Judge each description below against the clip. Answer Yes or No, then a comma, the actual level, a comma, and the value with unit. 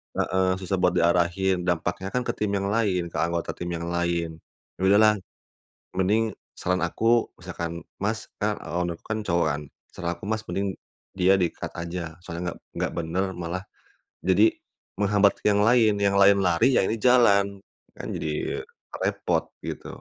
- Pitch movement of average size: Yes, average, 3.1 semitones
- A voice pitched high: No, very low, 95 Hz